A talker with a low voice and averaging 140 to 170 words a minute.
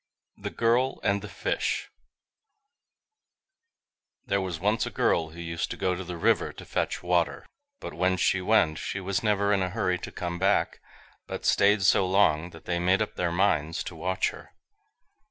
No: very low, 95 Hz; average, 180 wpm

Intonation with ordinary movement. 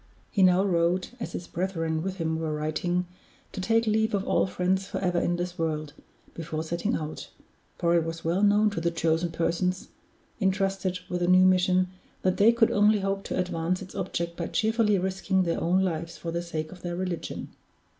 No: narrow, 2.3 semitones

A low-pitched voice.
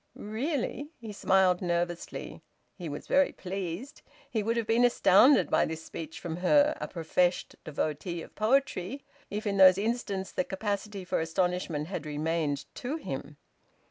No: high, 190 Hz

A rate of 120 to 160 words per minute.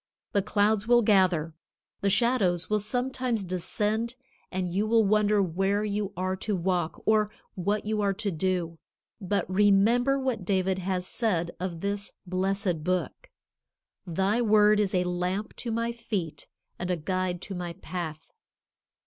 Yes: average, 150 wpm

